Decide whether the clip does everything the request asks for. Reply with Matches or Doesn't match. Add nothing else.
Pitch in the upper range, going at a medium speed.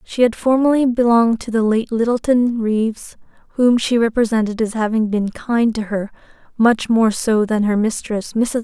Matches